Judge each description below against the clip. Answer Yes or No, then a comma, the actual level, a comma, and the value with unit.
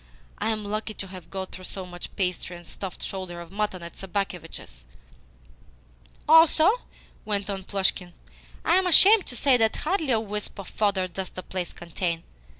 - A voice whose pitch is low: No, high, 195 Hz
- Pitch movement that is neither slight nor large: Yes, average, 3.3 semitones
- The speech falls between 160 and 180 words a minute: Yes, average, 170 wpm